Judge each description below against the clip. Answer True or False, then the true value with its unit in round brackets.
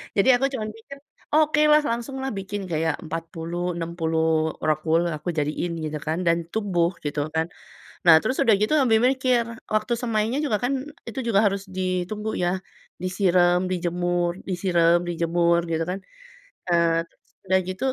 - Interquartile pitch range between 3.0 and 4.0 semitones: False (4.7 semitones)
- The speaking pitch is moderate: True (180 Hz)